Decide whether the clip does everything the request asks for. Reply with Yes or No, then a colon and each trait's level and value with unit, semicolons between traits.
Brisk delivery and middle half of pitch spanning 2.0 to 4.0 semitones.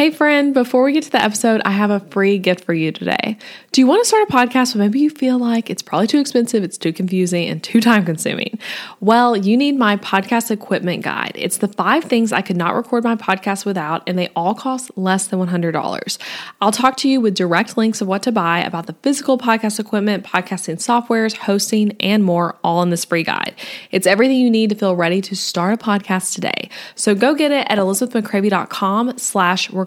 No: fast, 220 wpm; average, 4.5 semitones